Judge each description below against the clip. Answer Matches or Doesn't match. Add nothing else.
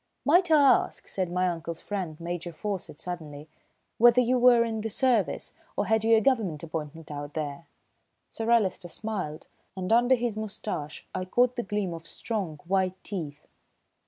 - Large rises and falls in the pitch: Matches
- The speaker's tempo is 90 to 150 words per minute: Doesn't match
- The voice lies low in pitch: Doesn't match